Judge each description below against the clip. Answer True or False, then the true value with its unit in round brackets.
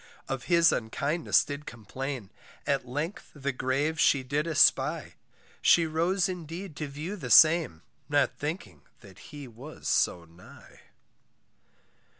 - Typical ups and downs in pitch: True (4.2 semitones)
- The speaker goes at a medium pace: False (130 wpm)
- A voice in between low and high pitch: True (145 Hz)